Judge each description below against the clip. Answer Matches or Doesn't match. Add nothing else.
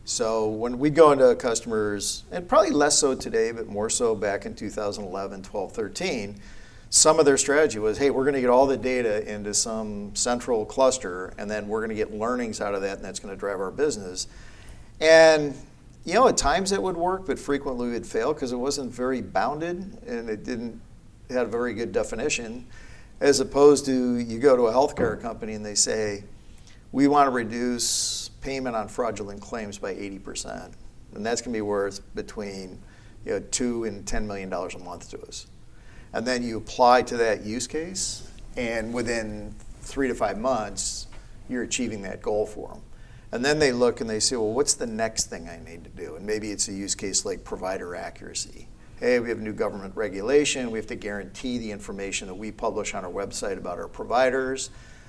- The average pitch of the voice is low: Matches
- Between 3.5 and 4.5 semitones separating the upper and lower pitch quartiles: Matches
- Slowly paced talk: Doesn't match